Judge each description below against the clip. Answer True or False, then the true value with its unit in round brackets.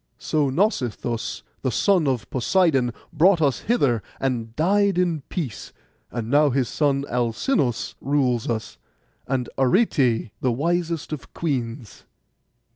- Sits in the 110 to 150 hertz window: True (135 Hz)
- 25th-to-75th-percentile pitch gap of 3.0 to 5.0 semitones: False (5.4 semitones)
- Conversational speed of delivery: False (120 wpm)